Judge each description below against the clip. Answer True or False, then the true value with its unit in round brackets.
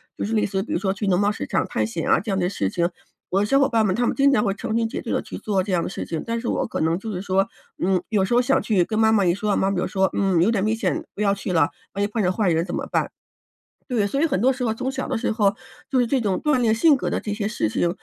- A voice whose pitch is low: False (205 Hz)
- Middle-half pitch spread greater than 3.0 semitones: True (3.4 semitones)